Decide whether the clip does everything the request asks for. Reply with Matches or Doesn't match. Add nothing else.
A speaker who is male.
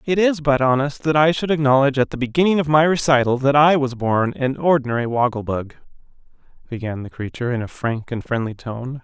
Matches